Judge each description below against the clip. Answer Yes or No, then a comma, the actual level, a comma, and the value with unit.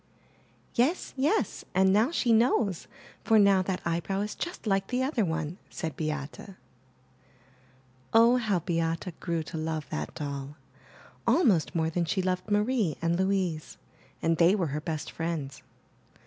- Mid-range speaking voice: Yes, medium, 180 Hz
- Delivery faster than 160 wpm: No, average, 150 wpm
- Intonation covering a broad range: No, average, 4.7 semitones